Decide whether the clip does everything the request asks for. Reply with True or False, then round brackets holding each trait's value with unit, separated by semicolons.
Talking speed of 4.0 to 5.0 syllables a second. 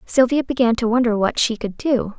False (5.3 syllables/s)